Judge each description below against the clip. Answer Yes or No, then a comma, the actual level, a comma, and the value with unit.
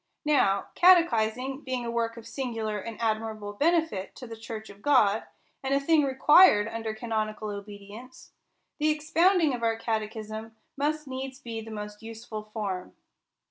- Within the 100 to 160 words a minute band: Yes, average, 150 wpm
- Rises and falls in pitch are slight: No, average, 4.0 semitones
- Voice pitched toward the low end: No, high, 225 Hz